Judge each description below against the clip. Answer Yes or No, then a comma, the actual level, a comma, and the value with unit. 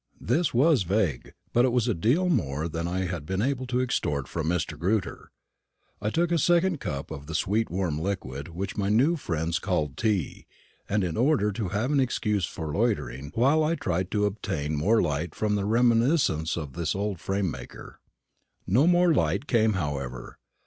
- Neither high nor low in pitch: No, low, 100 Hz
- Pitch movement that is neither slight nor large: No, wide, 7.1 semitones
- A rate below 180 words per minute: No, average, 185 wpm